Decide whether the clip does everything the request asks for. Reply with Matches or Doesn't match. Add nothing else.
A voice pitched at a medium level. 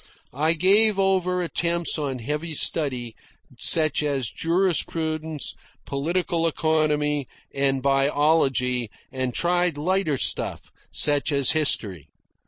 Matches